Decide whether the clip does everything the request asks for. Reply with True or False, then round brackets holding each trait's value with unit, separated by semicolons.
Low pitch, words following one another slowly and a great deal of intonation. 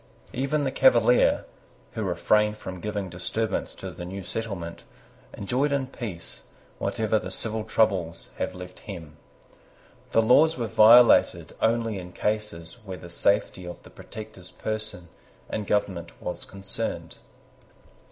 False (105 Hz; 130 wpm; 3.7 semitones)